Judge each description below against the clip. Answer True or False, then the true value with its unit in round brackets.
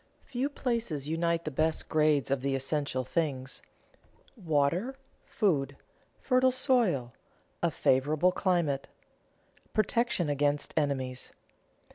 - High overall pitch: False (155 Hz)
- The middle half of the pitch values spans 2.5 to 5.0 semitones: False (5.6 semitones)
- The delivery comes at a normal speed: False (100 wpm)